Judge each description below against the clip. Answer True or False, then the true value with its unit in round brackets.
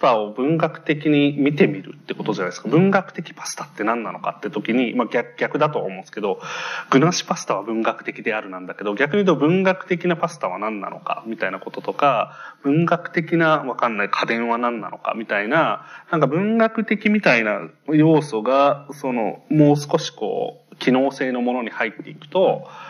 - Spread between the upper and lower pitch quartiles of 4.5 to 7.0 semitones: True (5.6 semitones)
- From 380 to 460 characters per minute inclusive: True (390 characters per minute)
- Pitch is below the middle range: False (150 Hz)